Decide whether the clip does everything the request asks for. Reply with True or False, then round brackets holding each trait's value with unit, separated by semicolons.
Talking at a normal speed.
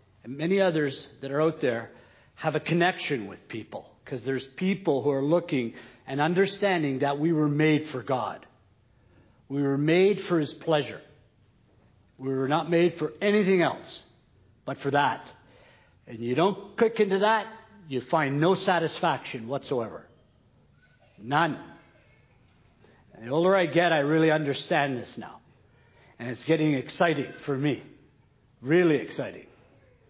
True (145 wpm)